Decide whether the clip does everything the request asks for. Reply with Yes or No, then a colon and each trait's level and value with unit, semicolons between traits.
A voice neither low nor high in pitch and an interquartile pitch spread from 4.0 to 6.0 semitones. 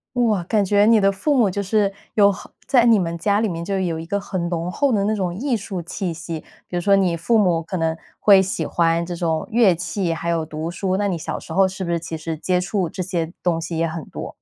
No: medium, 180 Hz; average, 3.2 semitones